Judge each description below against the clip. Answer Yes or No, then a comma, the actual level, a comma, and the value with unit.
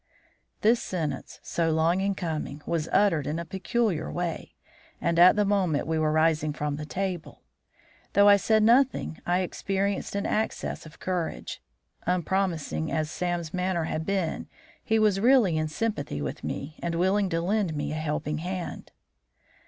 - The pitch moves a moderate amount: Yes, average, 3.8 semitones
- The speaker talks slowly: No, average, 160 wpm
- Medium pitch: Yes, medium, 175 Hz